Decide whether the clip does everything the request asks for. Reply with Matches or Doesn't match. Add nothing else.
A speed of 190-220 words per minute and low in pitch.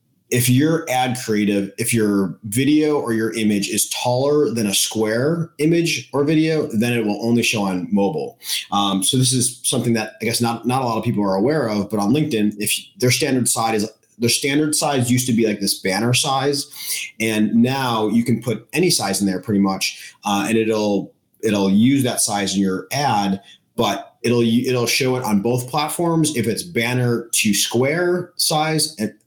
Matches